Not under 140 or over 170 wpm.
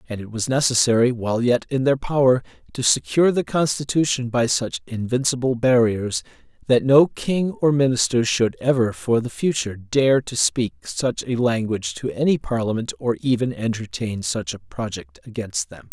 Yes: average, 165 wpm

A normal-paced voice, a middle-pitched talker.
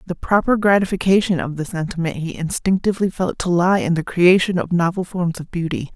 Yes: average, 190 wpm; medium, 180 Hz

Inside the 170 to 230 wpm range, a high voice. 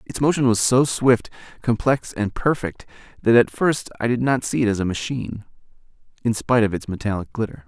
No: average, 195 wpm; low, 115 Hz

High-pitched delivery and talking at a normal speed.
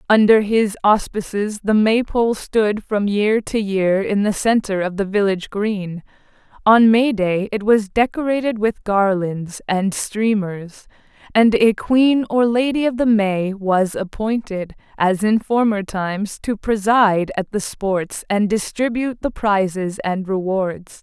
Yes: high, 210 Hz; average, 150 wpm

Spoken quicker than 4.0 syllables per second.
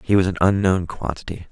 Yes: 5.8 syllables/s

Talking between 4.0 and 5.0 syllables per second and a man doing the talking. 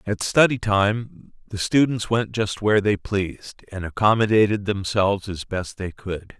Yes: 4.4 syllables/s; male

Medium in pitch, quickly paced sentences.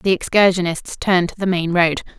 No: medium, 180 Hz; average, 190 wpm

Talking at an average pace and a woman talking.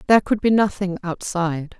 Yes: average, 165 wpm; female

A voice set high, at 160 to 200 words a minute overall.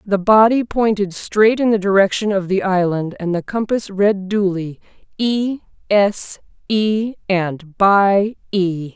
No: high, 200 Hz; average, 140 wpm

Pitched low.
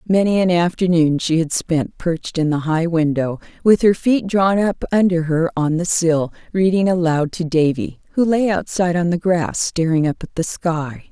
No: medium, 170 Hz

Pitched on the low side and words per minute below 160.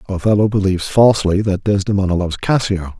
Yes: low, 100 Hz; average, 140 wpm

